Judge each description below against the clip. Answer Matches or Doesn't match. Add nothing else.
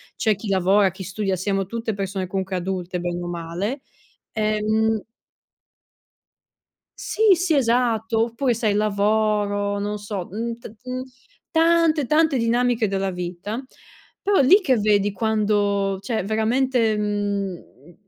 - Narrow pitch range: Doesn't match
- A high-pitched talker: Matches